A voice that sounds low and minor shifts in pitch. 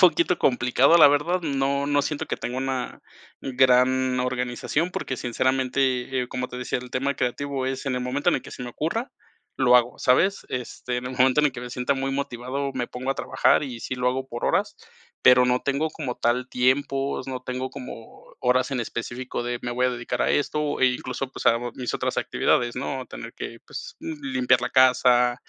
Yes: low, 130 Hz; narrow, 1.8 semitones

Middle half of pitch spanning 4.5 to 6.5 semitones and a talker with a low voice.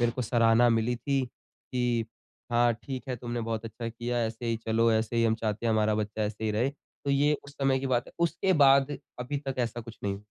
No: average, 2.7 semitones; low, 120 Hz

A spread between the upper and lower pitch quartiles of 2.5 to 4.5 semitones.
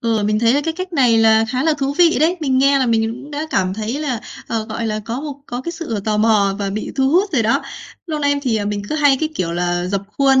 No: average, 5.1 semitones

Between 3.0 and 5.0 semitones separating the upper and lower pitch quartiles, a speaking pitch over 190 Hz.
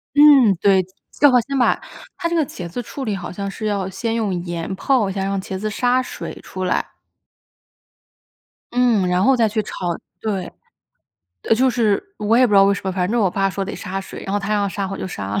Yes: average, 4.0 semitones; high, 205 Hz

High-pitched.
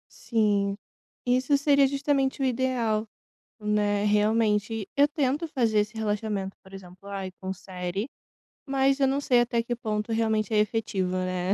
Yes: high, 220 Hz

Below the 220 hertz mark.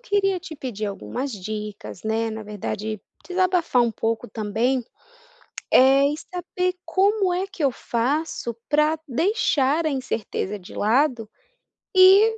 No: very high, 270 Hz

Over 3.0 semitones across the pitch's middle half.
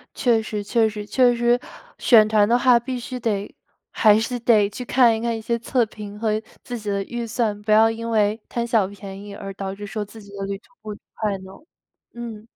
No: narrow, 2.4 semitones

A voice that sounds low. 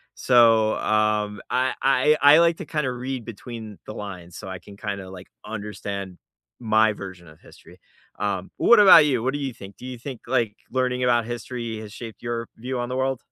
Yes: low, 115 Hz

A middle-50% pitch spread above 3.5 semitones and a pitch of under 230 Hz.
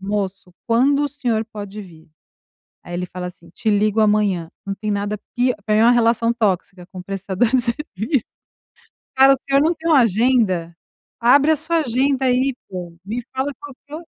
Yes: average, 5.1 semitones; high, 220 Hz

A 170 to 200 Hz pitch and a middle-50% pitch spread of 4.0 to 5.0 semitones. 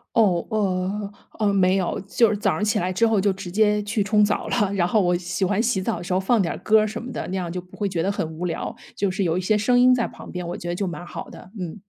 No: high, 195 Hz; average, 2.8 semitones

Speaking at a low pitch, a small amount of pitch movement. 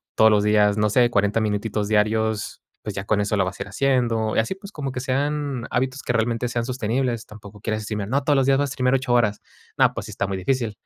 No: low, 115 Hz; average, 3.7 semitones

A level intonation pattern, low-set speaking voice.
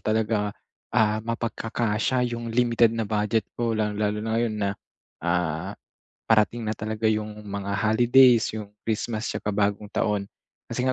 Yes: narrow, 1.8 semitones; low, 110 Hz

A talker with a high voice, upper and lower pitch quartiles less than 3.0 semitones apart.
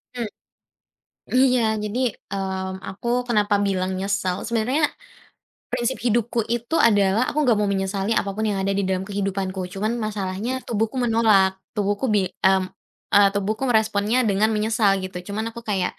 Yes: high, 205 Hz; narrow, 2.6 semitones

